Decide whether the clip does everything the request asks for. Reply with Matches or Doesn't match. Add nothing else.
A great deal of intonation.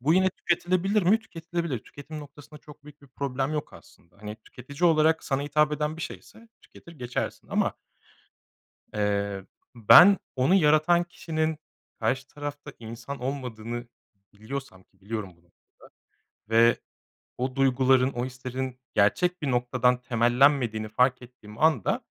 Doesn't match